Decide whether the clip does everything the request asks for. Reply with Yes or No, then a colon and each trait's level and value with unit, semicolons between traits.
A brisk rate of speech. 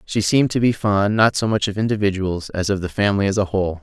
Yes: fast, 265 wpm